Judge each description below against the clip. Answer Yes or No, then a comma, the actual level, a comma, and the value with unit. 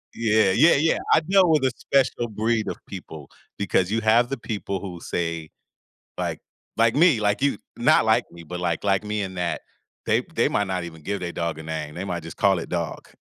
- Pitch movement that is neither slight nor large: Yes, average, 5.0 semitones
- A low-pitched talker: Yes, low, 100 Hz